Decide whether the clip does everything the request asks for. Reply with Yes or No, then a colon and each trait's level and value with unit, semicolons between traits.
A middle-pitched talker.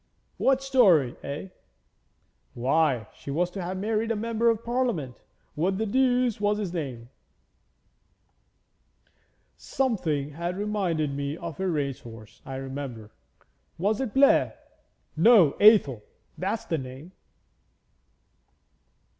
Yes: medium, 175 Hz